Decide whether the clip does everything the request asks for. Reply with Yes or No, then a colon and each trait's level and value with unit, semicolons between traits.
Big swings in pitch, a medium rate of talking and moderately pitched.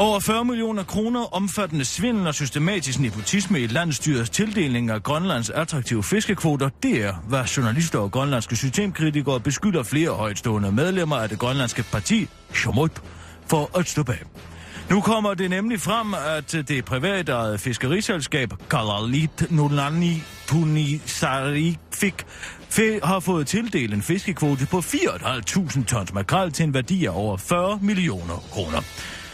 No: wide, 7.8 semitones; slow, 135 wpm; medium, 150 Hz